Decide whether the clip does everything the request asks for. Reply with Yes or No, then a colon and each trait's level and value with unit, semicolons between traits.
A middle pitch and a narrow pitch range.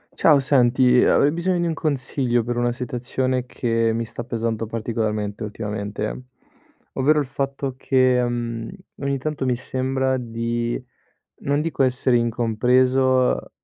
No: low, 125 Hz; narrow, 2.3 semitones